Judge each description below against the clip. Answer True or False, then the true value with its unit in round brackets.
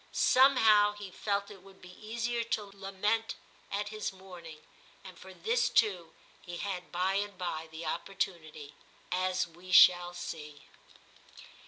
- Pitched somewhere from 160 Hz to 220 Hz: True (190 Hz)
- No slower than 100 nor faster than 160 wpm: True (140 wpm)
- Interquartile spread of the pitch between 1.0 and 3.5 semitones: True (2.9 semitones)